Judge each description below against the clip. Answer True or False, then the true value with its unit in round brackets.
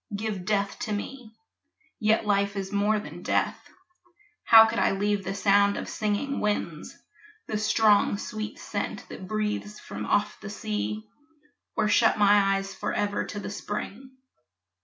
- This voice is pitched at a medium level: False (205 Hz)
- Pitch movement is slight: True (1.4 semitones)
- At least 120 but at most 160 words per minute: True (150 wpm)